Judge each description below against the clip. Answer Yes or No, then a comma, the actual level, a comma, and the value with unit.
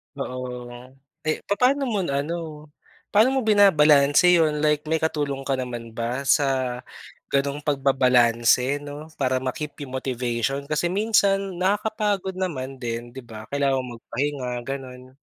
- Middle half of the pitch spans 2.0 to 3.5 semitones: No, average, 4.3 semitones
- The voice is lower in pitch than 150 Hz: Yes, medium, 140 Hz